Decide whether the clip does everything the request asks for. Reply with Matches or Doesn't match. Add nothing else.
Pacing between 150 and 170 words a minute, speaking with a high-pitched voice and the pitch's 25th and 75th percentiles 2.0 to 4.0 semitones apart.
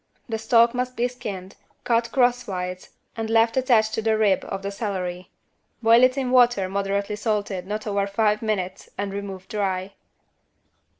Matches